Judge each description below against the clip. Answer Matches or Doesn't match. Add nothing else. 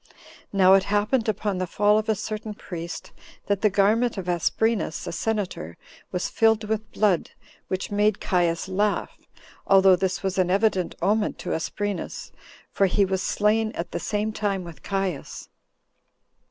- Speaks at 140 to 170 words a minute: Matches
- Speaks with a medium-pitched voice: Doesn't match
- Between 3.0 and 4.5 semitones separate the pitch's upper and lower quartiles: Doesn't match